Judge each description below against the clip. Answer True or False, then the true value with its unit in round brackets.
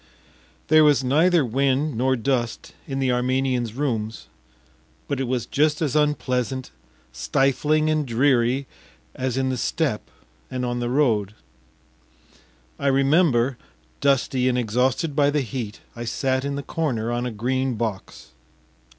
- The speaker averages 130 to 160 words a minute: True (140 wpm)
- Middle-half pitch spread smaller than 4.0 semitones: True (2.7 semitones)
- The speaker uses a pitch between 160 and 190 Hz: False (130 Hz)